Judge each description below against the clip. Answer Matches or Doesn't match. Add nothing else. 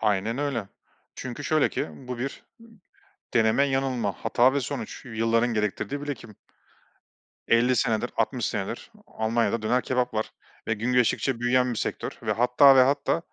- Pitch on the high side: Doesn't match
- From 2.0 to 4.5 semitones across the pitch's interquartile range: Matches